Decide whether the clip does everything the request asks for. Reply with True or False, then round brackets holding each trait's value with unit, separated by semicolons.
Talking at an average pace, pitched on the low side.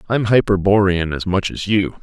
True (175 wpm; 95 Hz)